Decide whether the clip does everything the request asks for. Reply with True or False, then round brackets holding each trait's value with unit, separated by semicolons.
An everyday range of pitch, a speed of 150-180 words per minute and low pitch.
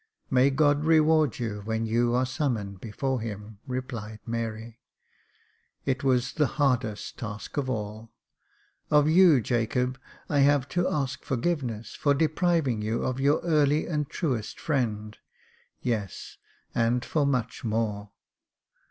False (4.4 semitones; 140 wpm; 125 Hz)